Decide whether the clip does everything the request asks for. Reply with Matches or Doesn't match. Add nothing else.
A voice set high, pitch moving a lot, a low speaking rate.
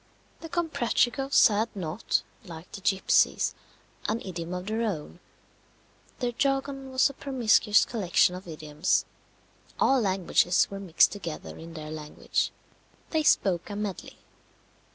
Matches